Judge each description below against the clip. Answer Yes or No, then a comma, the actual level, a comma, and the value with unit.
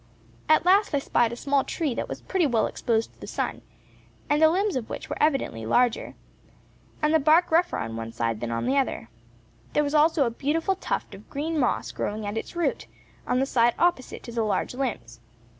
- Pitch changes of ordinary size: No, wide, 6.0 semitones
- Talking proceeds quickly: Yes, fast, 210 wpm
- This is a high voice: Yes, very high, 270 Hz